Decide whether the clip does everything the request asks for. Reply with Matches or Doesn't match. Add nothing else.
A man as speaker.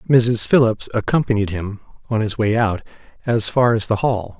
Matches